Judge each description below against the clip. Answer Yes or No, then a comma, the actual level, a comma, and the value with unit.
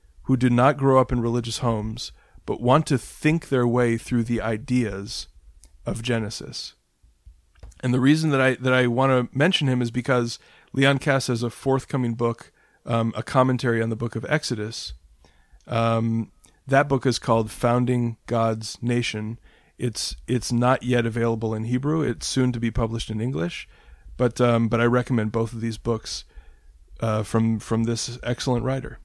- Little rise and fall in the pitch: Yes, narrow, 2.1 semitones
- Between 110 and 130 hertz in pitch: Yes, low, 120 Hz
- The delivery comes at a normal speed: No, fast, 170 wpm